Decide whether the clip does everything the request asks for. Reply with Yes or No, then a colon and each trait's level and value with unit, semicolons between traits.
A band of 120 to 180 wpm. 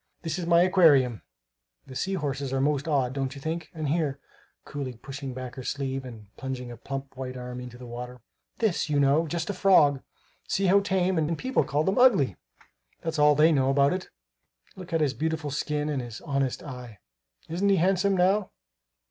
No: average, 195 wpm